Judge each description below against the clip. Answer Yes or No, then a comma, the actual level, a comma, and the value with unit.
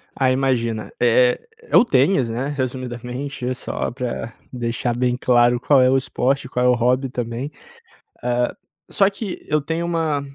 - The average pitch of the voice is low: Yes, low, 125 Hz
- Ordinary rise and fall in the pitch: No, narrow, 2.2 semitones